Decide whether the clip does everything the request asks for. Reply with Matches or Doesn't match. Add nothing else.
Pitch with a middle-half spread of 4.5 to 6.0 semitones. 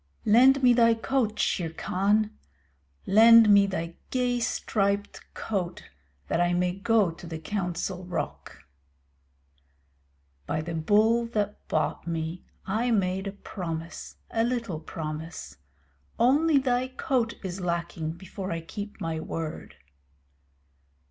Matches